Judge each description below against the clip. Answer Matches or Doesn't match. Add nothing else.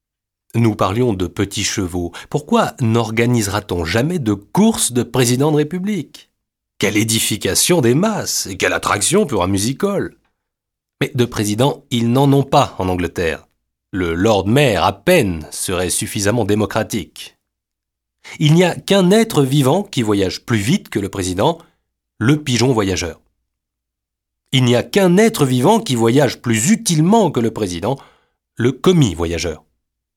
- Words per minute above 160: Doesn't match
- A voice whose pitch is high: Doesn't match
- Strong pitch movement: Matches